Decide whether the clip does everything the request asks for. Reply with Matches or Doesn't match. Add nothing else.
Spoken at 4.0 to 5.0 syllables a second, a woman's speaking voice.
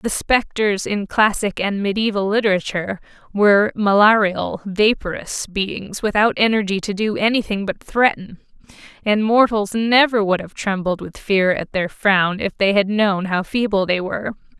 Matches